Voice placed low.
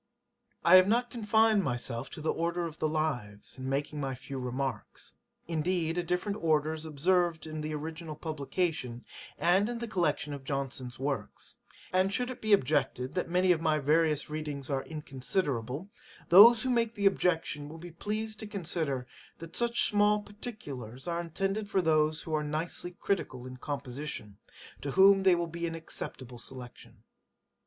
No: medium, 160 Hz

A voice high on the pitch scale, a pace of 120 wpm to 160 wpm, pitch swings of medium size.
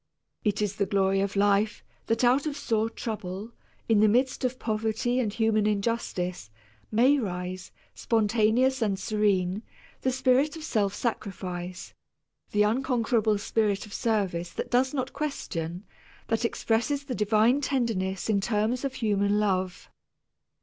Yes: high, 215 Hz; average, 140 wpm; average, 3.5 semitones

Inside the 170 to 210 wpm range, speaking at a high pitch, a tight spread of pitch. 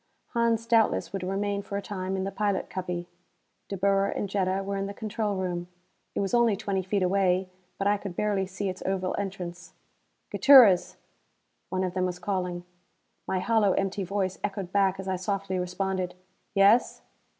Yes: average, 175 wpm; high, 195 Hz; narrow, 1.5 semitones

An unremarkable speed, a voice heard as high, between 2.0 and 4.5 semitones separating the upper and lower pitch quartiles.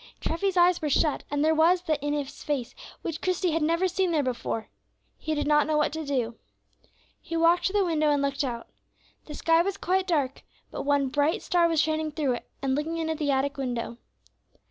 No: fast, 215 wpm; very high, 310 Hz; average, 3.0 semitones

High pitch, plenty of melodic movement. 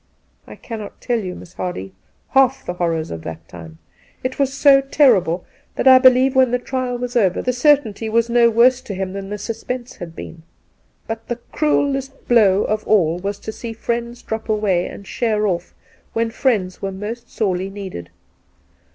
No: high, 225 Hz; average, 4.9 semitones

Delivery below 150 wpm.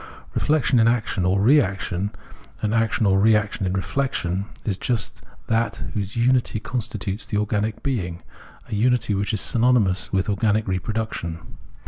Yes: average, 140 wpm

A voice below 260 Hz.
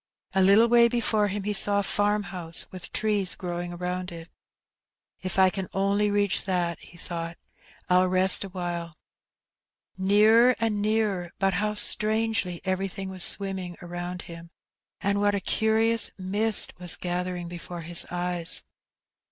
Yes: high, 190 Hz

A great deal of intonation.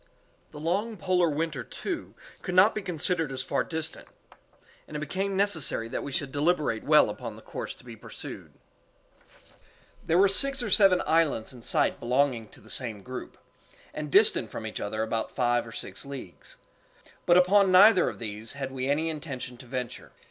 Yes: wide, 6.7 semitones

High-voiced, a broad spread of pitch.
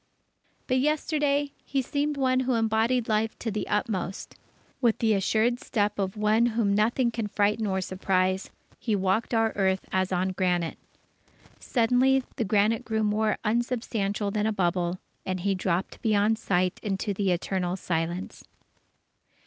No: high, 210 Hz; average, 3.5 semitones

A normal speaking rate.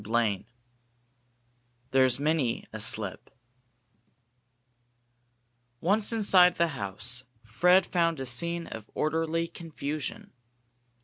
No: slow, 100 wpm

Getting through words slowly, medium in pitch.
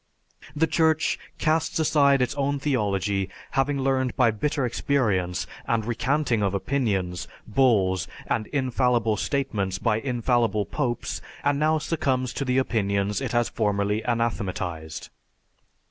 No: slow, 125 wpm; low, 120 Hz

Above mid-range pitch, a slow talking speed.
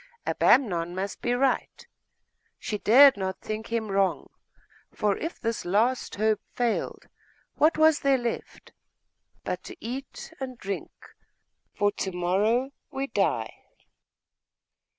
Yes: high, 225 Hz; slow, 120 wpm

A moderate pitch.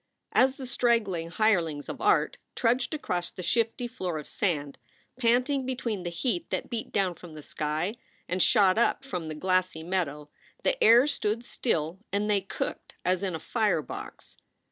No: high, 195 Hz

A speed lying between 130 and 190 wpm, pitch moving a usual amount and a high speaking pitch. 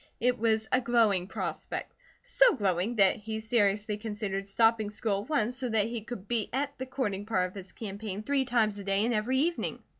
No: fast, 205 wpm; average, 3.1 semitones; high, 220 Hz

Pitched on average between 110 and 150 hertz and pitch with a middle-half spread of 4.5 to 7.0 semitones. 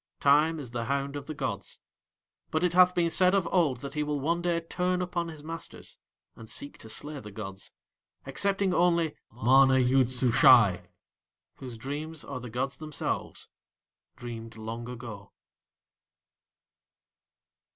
Yes: medium, 140 Hz; average, 5.3 semitones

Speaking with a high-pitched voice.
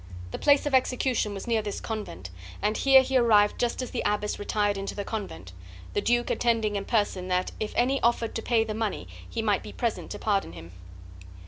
Yes: high, 215 Hz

